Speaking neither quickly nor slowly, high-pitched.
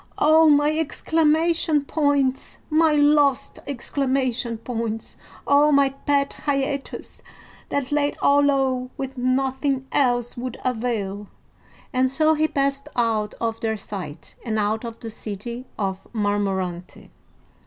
No: slow, 120 wpm; very high, 260 Hz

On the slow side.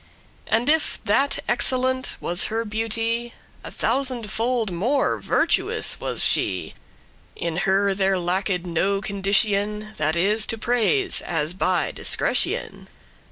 Yes: slow, 130 wpm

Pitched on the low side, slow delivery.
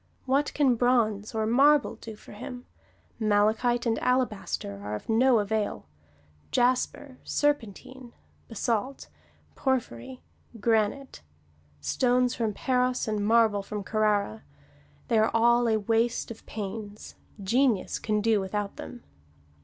No: high, 225 Hz; slow, 120 wpm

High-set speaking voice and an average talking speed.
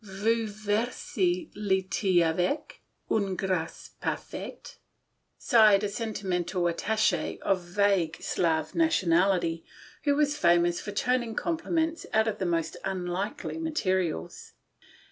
No: high, 195 Hz; slow, 120 wpm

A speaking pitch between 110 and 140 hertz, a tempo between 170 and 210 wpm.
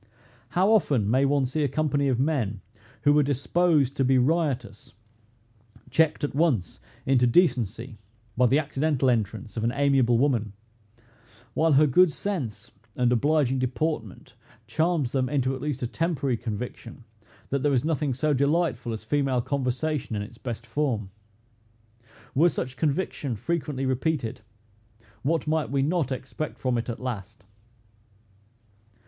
No: low, 135 Hz; average, 145 wpm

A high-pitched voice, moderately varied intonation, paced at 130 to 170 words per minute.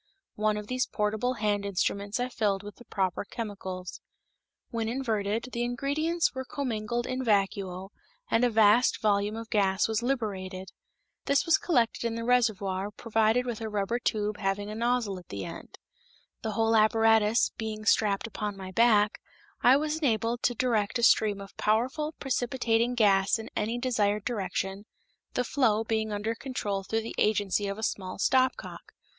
Yes: high, 220 Hz; average, 3.0 semitones; average, 165 wpm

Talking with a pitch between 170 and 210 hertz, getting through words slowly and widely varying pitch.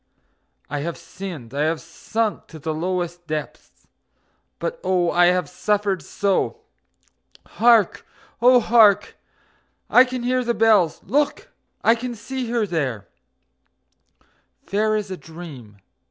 Yes: high, 190 Hz; slow, 125 wpm; wide, 5.7 semitones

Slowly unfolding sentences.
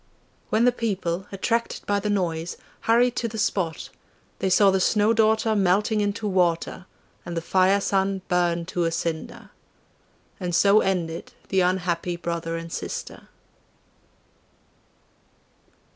Yes: slow, 130 wpm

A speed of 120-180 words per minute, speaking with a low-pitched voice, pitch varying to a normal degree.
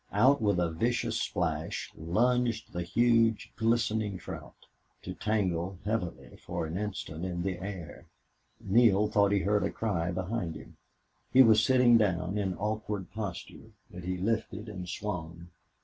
Yes: average, 150 wpm; low, 100 Hz; average, 3.9 semitones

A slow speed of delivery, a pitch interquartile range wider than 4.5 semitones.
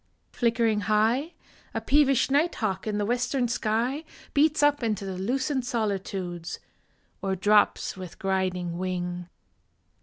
Yes: slow, 125 wpm; average, 5.1 semitones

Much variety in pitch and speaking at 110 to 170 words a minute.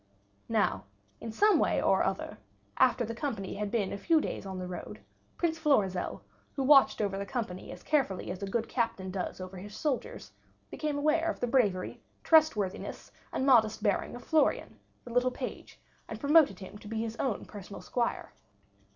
No: wide, 5.9 semitones; average, 180 wpm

